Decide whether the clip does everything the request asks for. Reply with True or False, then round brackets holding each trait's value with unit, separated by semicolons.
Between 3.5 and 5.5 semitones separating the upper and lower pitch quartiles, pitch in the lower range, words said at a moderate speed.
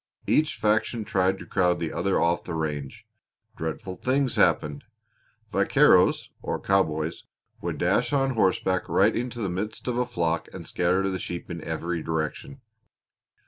True (5.0 semitones; 95 Hz; 150 wpm)